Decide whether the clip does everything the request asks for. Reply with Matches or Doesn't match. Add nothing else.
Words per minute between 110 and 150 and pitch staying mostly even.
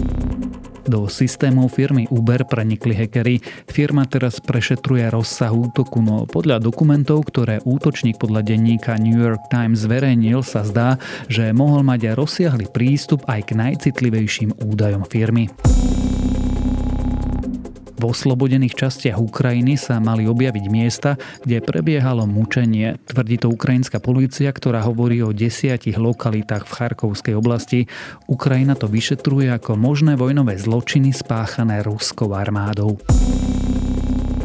Doesn't match